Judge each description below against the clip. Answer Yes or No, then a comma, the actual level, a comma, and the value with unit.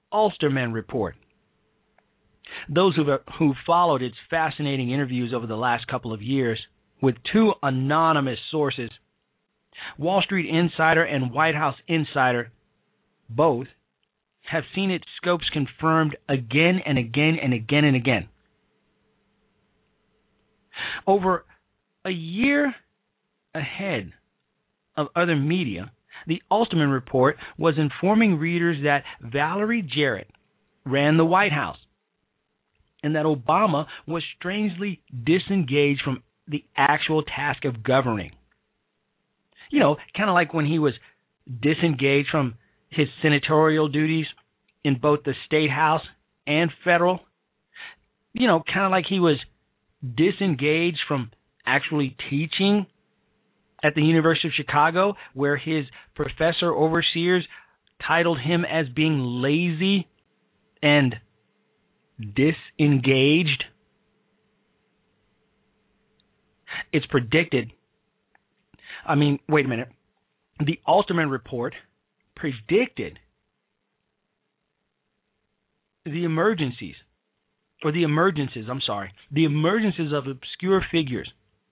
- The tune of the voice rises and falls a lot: No, average, 4.2 semitones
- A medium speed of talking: No, slow, 105 wpm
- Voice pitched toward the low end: No, medium, 155 Hz